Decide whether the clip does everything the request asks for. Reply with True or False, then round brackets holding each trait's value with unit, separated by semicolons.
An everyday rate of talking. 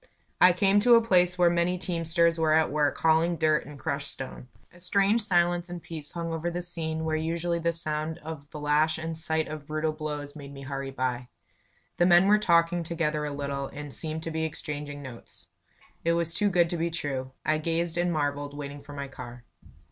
False (210 wpm)